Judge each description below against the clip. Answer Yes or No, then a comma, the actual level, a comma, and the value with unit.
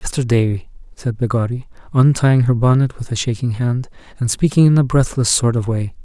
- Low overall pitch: Yes, low, 120 Hz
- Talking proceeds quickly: No, average, 190 wpm